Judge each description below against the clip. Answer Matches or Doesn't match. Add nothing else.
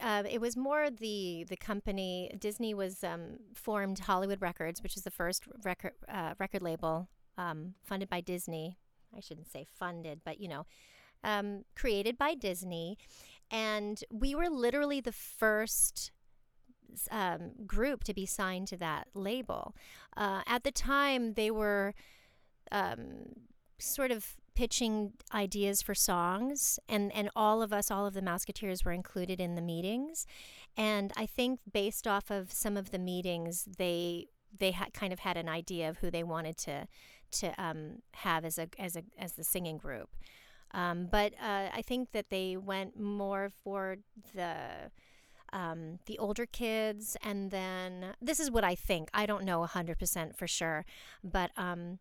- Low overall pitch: Doesn't match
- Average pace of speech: Matches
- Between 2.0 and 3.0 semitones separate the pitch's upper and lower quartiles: Doesn't match